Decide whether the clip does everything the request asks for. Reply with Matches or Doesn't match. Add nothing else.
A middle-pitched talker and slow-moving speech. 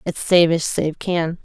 Doesn't match